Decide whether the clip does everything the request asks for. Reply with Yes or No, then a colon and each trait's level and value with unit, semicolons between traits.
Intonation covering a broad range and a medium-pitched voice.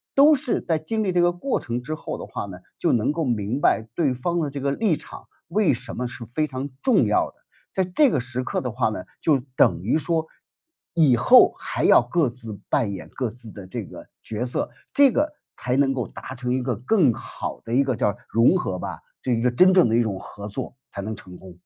No: wide, 6.2 semitones; low, 130 Hz